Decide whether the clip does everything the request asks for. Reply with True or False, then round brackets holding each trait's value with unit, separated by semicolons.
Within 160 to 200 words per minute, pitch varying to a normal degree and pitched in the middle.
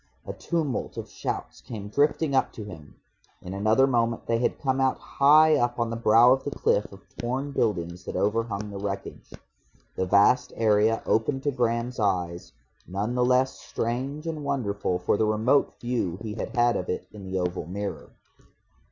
False (180 wpm; 4.5 semitones; 115 Hz)